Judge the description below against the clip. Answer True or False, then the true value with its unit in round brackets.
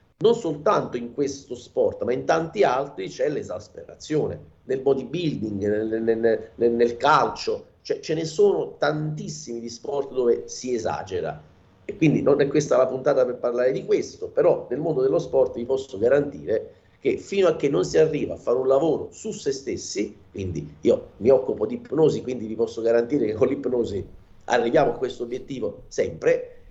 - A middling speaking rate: False (180 wpm)